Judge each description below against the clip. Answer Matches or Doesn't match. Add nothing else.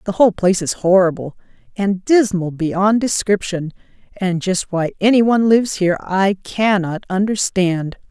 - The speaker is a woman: Matches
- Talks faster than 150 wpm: Doesn't match